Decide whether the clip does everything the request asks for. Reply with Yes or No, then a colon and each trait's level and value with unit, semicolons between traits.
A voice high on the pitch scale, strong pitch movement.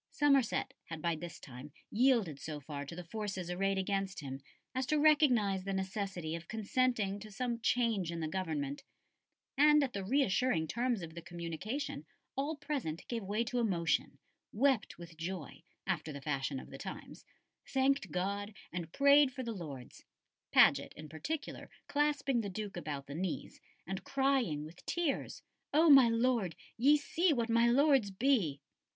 Yes: high, 200 Hz; wide, 7.6 semitones